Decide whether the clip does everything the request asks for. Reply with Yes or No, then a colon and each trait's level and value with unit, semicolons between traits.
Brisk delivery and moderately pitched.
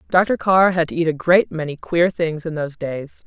Yes: fast, 240 wpm; medium, 165 Hz